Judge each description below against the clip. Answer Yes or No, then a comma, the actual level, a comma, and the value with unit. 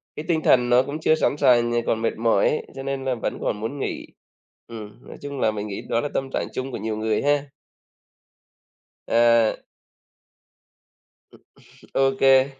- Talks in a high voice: No, low, 125 Hz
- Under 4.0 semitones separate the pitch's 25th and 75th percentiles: Yes, average, 3.4 semitones